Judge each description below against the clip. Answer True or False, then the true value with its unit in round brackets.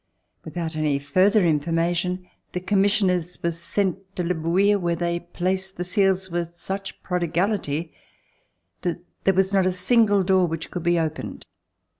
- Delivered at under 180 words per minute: True (155 wpm)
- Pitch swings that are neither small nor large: False (2.2 semitones)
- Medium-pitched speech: True (180 Hz)